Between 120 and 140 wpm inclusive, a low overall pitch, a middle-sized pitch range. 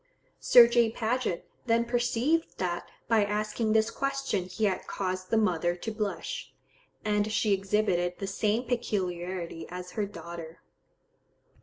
No: slow, 135 wpm; high, 210 Hz; average, 4.1 semitones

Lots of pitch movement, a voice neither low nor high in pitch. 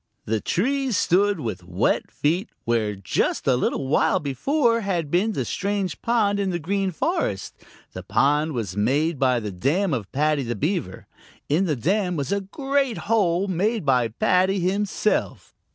Yes: wide, 7.3 semitones; medium, 175 Hz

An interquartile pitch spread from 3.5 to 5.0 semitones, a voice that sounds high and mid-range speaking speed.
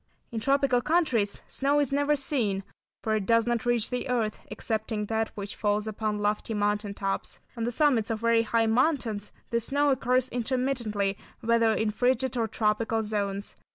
No: average, 3.0 semitones; high, 230 Hz; average, 170 wpm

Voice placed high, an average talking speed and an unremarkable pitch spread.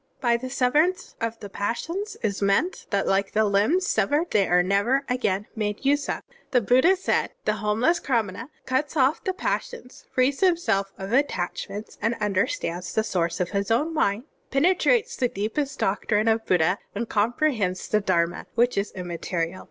No: high, 225 Hz; average, 170 wpm; wide, 5.9 semitones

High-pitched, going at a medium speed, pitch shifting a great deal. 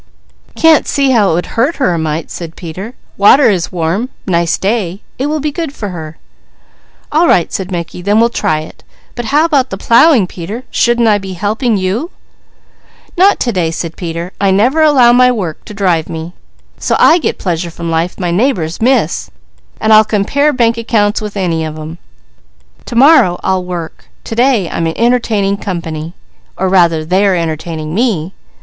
Yes: high, 195 Hz; average, 180 wpm; wide, 5.9 semitones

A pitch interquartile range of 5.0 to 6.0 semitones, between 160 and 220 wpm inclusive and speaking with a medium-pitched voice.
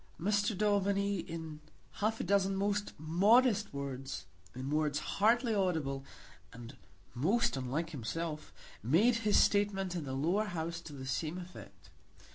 No: wide, 5.6 semitones; slow, 135 wpm; medium, 175 Hz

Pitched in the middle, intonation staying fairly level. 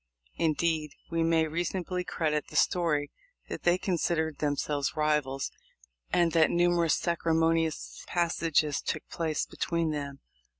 Yes: medium, 160 Hz; narrow, 2.0 semitones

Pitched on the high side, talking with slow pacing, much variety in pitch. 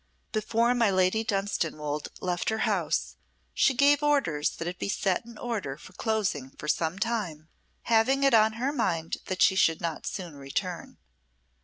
No: high, 195 Hz; average, 165 wpm; wide, 5.9 semitones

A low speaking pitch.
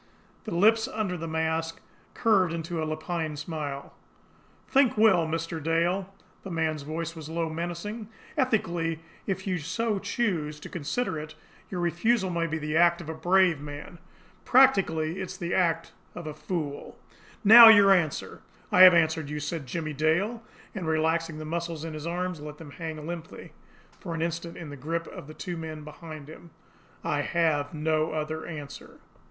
No: medium, 165 Hz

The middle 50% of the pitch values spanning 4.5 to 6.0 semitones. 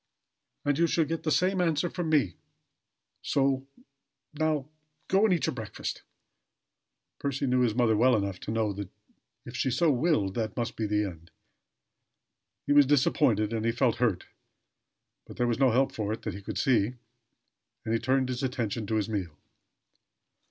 Yes: average, 4.8 semitones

